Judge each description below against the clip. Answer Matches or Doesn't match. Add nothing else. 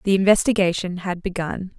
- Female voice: Matches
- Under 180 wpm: Matches